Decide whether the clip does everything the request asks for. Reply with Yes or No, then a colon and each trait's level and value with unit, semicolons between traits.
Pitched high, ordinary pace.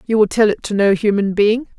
No: high, 210 Hz; fast, 270 wpm